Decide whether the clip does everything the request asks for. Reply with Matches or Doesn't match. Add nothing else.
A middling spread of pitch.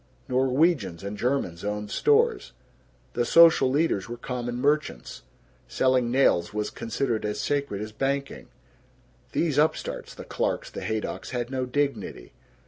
Matches